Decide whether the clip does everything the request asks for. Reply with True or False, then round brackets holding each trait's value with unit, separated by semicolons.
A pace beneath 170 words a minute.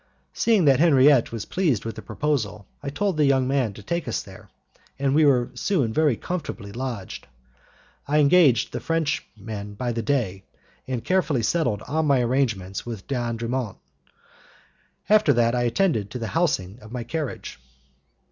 True (160 wpm)